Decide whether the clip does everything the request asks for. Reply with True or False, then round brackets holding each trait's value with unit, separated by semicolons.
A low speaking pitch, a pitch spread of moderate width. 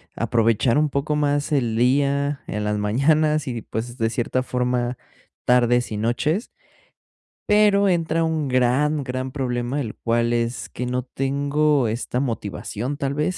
True (130 Hz; 3.7 semitones)